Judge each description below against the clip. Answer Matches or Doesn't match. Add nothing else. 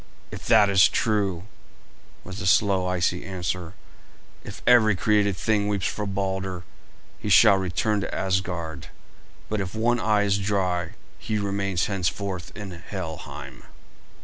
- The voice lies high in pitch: Doesn't match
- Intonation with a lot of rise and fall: Doesn't match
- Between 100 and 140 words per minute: Matches